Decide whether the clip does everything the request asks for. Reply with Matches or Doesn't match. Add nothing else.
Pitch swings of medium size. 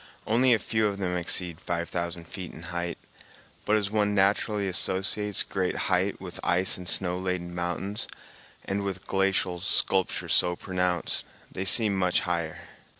Doesn't match